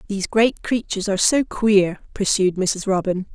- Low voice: No, high, 200 Hz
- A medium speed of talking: Yes, average, 160 wpm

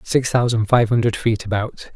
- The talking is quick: No, average, 185 wpm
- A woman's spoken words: No, male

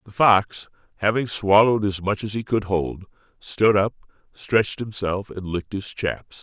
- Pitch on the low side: Yes, low, 100 Hz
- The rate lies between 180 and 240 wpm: No, average, 170 wpm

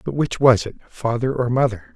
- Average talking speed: No, fast, 215 wpm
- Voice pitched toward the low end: Yes, low, 120 Hz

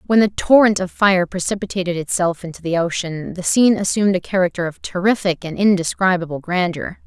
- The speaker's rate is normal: Yes, average, 170 wpm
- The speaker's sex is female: Yes, female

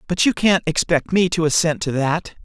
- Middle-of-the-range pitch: Yes, medium, 170 Hz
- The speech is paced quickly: Yes, fast, 220 wpm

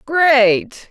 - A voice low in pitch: No, very high, 260 Hz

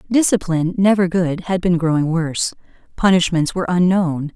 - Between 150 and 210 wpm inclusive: No, average, 140 wpm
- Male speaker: No, female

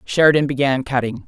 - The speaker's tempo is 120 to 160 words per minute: Yes, average, 140 wpm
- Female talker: Yes, female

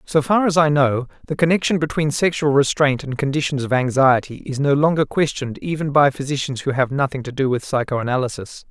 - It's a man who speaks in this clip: Yes, male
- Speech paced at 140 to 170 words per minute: No, average, 195 wpm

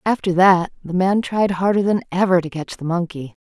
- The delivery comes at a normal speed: No, fast, 210 wpm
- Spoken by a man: No, female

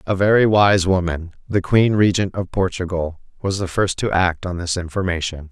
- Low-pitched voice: Yes, very low, 95 Hz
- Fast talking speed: No, average, 165 wpm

